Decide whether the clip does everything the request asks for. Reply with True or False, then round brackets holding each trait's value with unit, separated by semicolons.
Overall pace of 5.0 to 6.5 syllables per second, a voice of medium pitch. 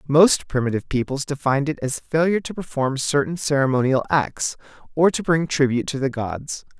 True (5.6 syllables/s; 145 Hz)